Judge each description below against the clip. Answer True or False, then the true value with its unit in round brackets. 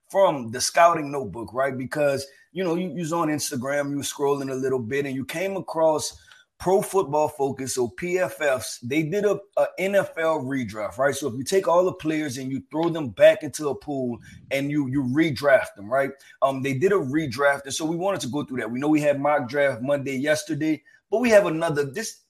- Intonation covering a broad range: False (3.8 semitones)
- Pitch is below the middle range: False (145 Hz)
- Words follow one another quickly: True (215 wpm)